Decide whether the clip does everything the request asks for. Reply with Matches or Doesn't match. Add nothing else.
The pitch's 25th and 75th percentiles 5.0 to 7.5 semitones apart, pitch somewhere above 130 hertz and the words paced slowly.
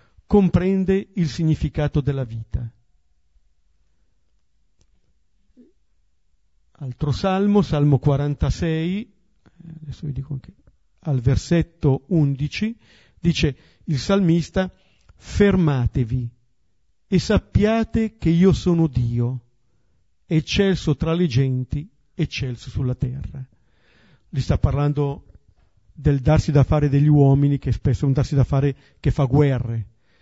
Matches